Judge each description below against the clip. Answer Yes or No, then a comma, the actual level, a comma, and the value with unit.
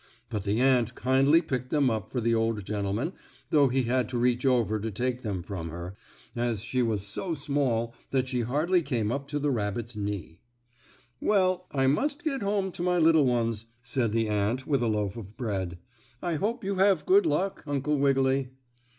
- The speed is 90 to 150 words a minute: No, average, 195 wpm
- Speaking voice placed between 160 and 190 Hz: No, low, 125 Hz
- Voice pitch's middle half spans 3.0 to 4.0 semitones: No, average, 5.1 semitones